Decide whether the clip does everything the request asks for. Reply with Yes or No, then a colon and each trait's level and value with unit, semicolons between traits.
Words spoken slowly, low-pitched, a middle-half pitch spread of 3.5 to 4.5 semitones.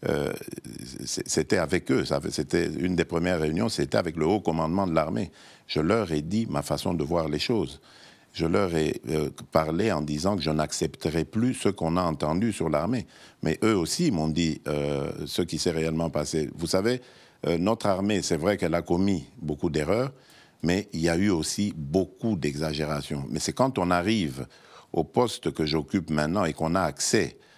No: average, 195 wpm; very low, 85 Hz; average, 4.1 semitones